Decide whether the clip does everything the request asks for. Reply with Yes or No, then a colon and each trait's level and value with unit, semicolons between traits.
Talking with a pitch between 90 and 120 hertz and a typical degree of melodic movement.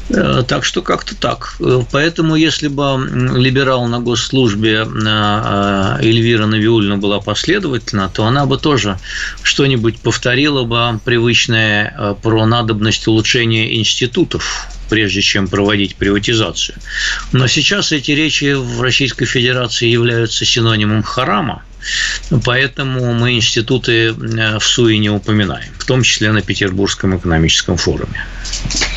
Yes: low, 115 Hz; average, 3.1 semitones